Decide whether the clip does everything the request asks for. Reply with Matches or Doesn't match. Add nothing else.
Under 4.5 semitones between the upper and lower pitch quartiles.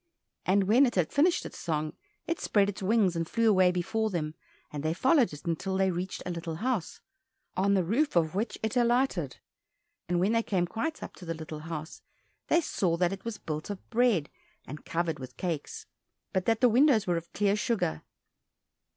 Doesn't match